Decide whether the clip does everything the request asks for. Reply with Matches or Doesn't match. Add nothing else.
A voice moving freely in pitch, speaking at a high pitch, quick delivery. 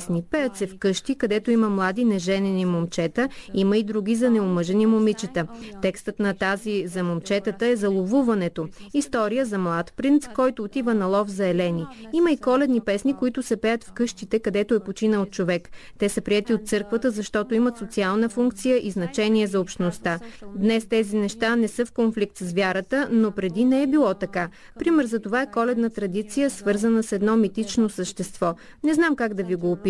Doesn't match